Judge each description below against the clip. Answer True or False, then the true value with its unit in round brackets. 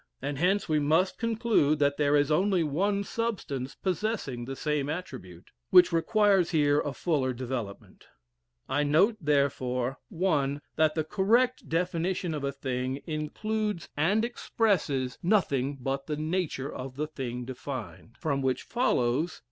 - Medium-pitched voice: True (150 Hz)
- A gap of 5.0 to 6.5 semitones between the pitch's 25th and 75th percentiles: True (5.4 semitones)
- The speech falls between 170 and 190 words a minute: False (145 wpm)